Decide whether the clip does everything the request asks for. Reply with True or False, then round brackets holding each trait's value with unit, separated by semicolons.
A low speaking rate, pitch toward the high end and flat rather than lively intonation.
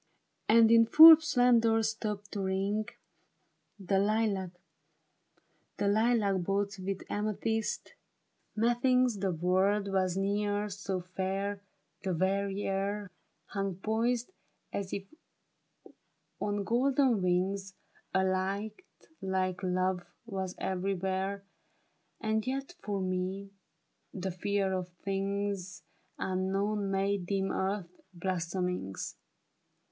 True (95 wpm; 195 Hz; 2.0 semitones)